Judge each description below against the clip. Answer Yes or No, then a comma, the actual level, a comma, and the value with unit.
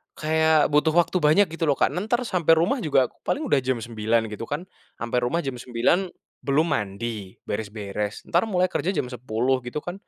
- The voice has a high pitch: No, medium, 140 Hz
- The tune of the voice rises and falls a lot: Yes, wide, 6.4 semitones